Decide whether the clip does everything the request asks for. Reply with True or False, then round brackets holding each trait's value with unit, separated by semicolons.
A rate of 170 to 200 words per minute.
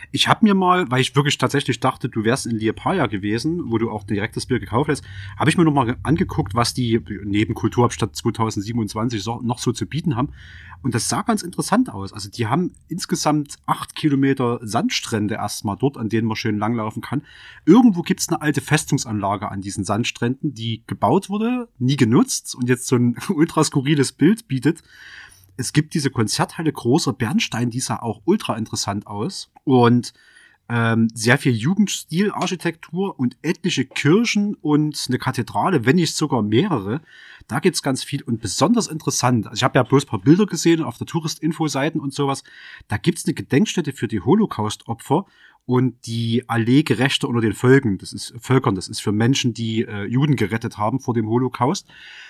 True (180 wpm)